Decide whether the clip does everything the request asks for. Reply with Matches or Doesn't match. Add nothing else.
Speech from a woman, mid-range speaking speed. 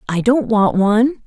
Matches